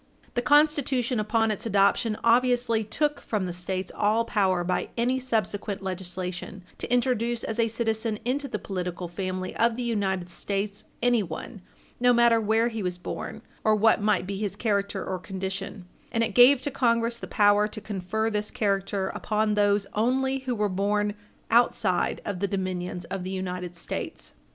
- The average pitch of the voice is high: Yes, high, 210 Hz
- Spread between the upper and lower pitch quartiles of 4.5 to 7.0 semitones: No, average, 3.6 semitones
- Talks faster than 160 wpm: Yes, average, 170 wpm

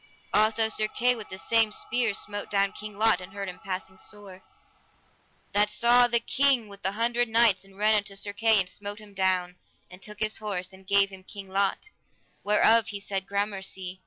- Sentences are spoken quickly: No, average, 195 wpm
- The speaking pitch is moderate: No, high, 205 Hz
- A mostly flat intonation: Yes, narrow, 2.3 semitones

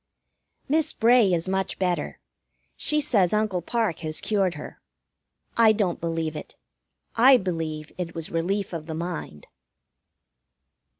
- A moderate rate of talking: No, slow, 130 wpm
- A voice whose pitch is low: No, medium, 180 Hz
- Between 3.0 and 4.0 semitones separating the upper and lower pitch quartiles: No, average, 4.7 semitones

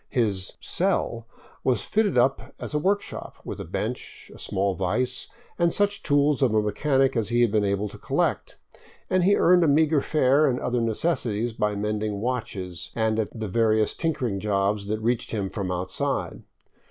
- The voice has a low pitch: Yes, low, 115 Hz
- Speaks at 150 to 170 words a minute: No, average, 190 wpm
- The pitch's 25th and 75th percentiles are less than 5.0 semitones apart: No, wide, 5.4 semitones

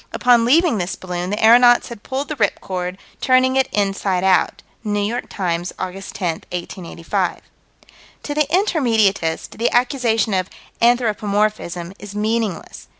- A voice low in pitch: No, high, 210 Hz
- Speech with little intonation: No, average, 4.6 semitones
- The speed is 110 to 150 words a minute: Yes, average, 140 wpm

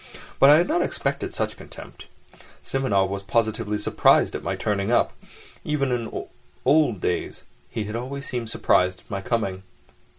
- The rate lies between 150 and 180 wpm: Yes, average, 160 wpm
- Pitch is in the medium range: No, low, 115 Hz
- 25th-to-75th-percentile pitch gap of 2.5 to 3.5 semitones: No, average, 5.2 semitones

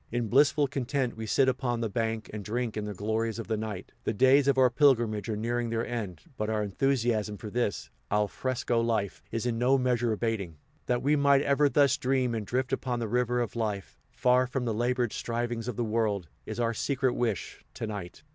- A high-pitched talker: No, low, 120 Hz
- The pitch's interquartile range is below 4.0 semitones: Yes, average, 2.8 semitones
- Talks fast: Yes, fast, 215 wpm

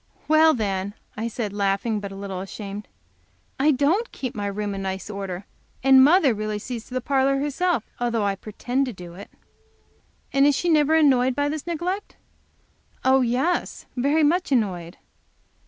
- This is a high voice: Yes, high, 245 Hz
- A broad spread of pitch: Yes, wide, 6.3 semitones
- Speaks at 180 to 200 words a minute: No, average, 170 wpm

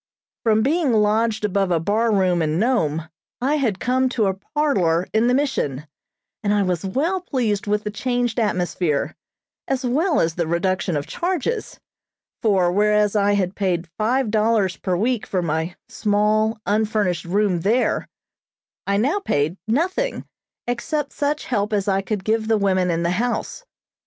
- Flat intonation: No, average, 4.9 semitones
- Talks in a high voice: Yes, high, 210 Hz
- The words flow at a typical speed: Yes, average, 160 wpm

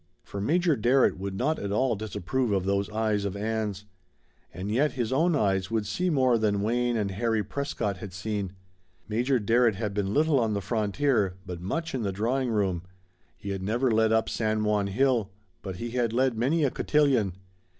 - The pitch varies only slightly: No, average, 4.1 semitones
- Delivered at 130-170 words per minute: No, average, 190 wpm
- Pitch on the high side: No, low, 110 Hz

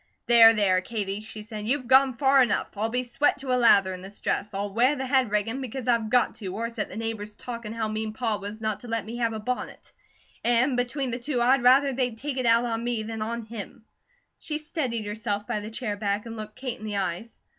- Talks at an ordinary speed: No, fast, 240 wpm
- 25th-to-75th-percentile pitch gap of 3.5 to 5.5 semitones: No, average, 2.9 semitones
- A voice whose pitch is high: Yes, high, 230 Hz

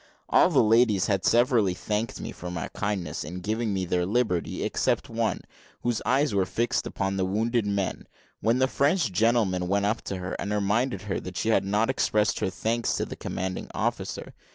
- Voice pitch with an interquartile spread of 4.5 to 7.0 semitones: No, average, 3.7 semitones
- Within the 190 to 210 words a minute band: Yes, average, 195 wpm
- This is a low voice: Yes, low, 105 Hz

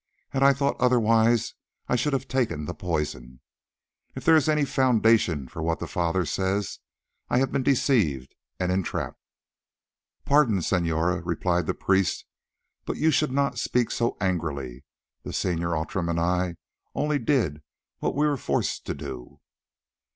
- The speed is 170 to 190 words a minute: No, average, 150 wpm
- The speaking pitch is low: Yes, very low, 95 Hz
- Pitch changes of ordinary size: No, wide, 7.9 semitones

